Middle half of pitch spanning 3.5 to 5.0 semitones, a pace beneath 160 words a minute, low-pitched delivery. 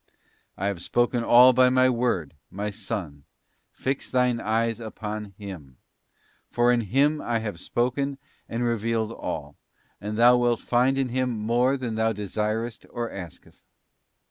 No: average, 2.8 semitones; average, 150 wpm; low, 115 Hz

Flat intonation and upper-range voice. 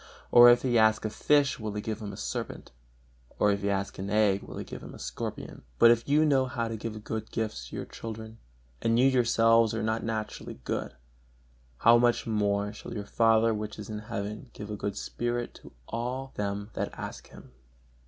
No: narrow, 2.1 semitones; low, 110 Hz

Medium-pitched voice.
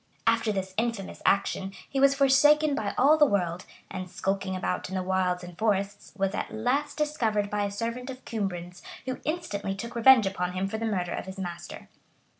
No: high, 205 Hz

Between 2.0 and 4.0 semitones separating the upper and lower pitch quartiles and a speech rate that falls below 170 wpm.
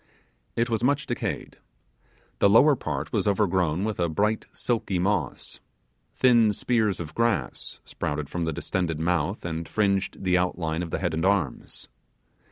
No: average, 4.8 semitones; average, 155 wpm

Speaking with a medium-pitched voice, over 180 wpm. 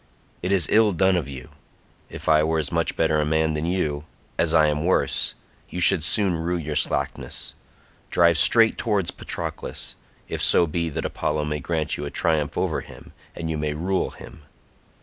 No: very low, 80 Hz; average, 190 wpm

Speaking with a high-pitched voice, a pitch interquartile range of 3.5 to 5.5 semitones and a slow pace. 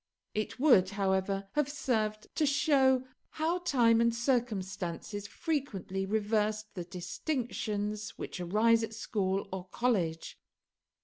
Yes: high, 215 Hz; average, 4.5 semitones; slow, 115 wpm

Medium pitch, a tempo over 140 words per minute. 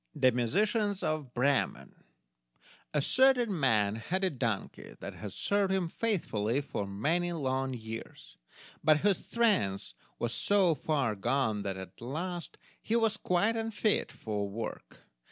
No: medium, 145 Hz; slow, 135 wpm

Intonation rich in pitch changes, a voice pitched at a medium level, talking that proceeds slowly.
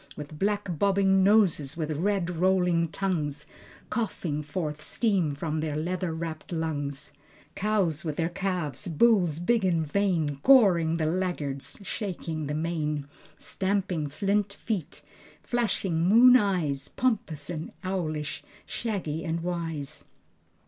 No: average, 4.1 semitones; medium, 170 Hz; slow, 120 wpm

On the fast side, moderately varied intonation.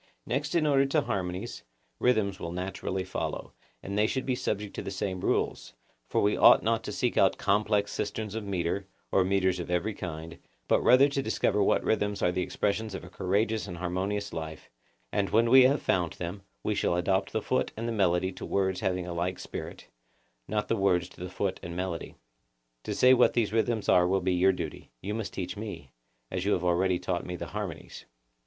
Yes: fast, 210 wpm; average, 3.2 semitones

